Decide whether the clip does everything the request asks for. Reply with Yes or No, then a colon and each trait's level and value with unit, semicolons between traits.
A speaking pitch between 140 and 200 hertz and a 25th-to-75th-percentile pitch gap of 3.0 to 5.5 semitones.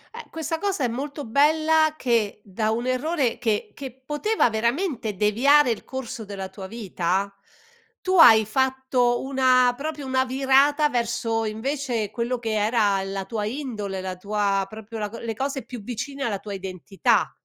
No: high, 240 Hz; average, 4.6 semitones